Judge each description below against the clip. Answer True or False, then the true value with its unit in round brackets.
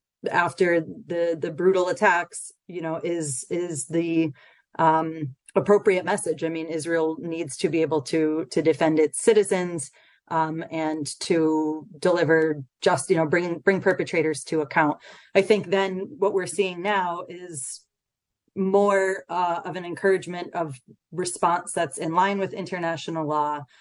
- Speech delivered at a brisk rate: False (145 wpm)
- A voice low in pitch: False (170 Hz)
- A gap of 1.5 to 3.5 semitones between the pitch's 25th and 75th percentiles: True (2.7 semitones)